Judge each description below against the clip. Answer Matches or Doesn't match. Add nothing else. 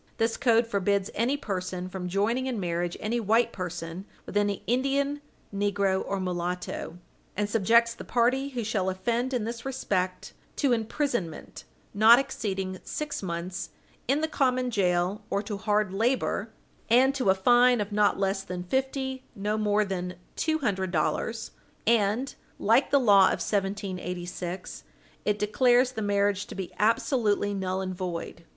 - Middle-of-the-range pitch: Doesn't match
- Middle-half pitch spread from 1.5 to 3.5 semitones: Doesn't match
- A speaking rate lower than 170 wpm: Matches